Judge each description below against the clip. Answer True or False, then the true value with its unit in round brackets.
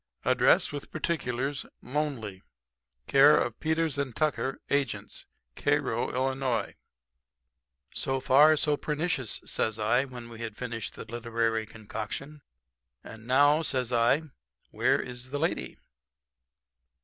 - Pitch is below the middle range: True (130 Hz)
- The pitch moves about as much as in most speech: True (3.9 semitones)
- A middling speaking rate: False (115 wpm)